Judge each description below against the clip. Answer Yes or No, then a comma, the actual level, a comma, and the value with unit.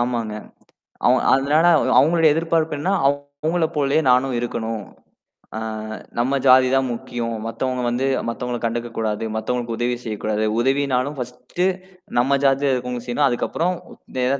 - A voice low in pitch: Yes, low, 125 Hz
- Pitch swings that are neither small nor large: Yes, average, 3.1 semitones